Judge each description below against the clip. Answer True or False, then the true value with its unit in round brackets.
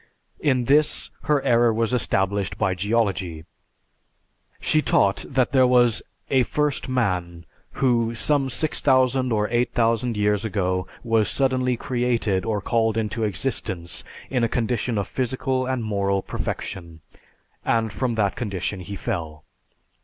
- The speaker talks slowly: True (130 wpm)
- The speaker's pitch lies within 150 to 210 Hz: False (115 Hz)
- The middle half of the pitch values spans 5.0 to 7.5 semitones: False (4.3 semitones)